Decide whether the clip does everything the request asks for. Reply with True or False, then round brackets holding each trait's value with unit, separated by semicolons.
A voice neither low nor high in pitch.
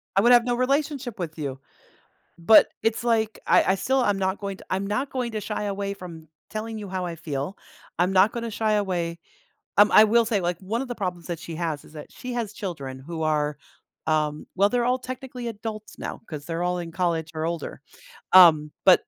False (195 Hz)